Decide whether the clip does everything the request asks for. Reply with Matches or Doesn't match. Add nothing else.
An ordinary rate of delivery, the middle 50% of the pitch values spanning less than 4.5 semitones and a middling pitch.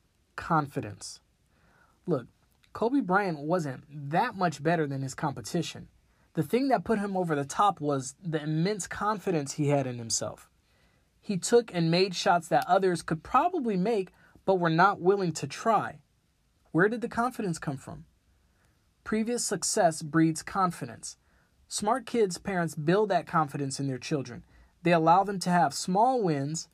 Doesn't match